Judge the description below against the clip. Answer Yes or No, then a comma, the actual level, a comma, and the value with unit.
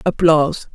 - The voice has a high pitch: No, medium, 160 Hz